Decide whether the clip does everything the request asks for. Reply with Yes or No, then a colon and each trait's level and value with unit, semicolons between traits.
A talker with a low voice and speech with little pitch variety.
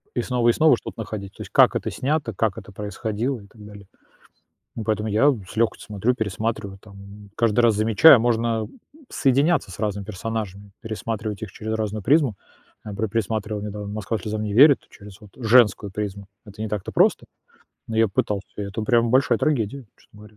Yes: low, 110 Hz; narrow, 2.2 semitones